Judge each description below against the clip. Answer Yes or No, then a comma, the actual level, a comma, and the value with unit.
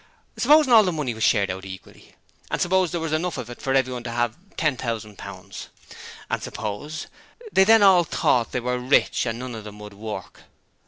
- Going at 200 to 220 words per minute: Yes, fast, 205 wpm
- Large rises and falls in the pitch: Yes, wide, 6.7 semitones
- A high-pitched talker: No, low, 125 Hz